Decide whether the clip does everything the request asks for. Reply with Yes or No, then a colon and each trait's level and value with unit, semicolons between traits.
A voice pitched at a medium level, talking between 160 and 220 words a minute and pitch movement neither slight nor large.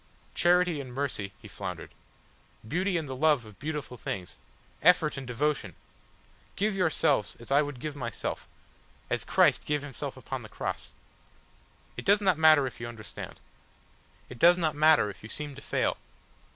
Yes: medium, 145 Hz; average, 165 wpm; average, 4.4 semitones